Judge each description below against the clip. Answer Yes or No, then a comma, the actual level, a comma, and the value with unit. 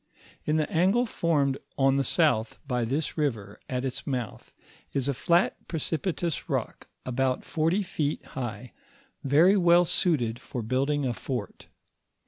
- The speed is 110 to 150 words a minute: Yes, average, 140 wpm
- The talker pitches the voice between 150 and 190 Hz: No, medium, 140 Hz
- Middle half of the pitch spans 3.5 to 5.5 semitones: Yes, average, 4.6 semitones